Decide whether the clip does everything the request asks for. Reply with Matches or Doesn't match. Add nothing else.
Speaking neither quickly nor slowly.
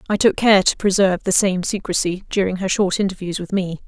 Doesn't match